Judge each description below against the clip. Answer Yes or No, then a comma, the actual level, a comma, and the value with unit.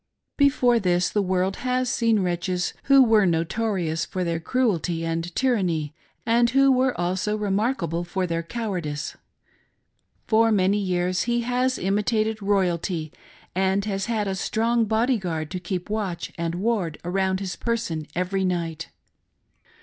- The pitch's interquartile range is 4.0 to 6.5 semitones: Yes, average, 4.5 semitones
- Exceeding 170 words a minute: No, average, 140 wpm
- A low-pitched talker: No, high, 195 Hz